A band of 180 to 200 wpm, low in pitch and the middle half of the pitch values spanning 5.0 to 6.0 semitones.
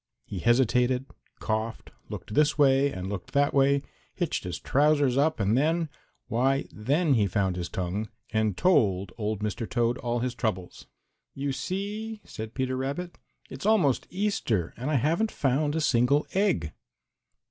No: average, 155 wpm; low, 130 Hz; wide, 5.4 semitones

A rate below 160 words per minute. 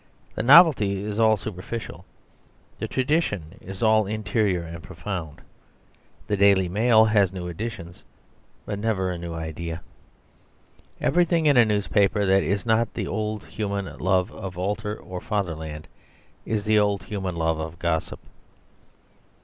Yes: average, 140 wpm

